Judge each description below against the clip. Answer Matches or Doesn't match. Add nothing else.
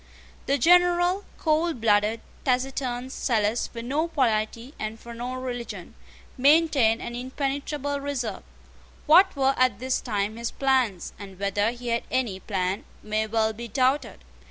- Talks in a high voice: Matches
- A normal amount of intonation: Matches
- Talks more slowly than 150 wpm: Matches